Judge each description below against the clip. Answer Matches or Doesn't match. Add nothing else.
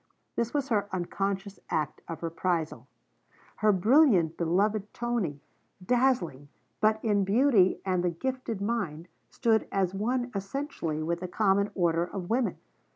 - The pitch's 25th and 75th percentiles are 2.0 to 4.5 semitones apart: Doesn't match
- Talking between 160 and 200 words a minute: Doesn't match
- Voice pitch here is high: Matches